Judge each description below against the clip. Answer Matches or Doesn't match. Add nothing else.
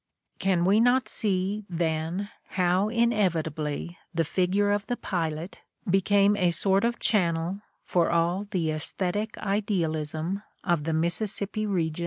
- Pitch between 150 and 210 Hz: Matches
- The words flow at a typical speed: Doesn't match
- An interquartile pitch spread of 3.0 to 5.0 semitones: Matches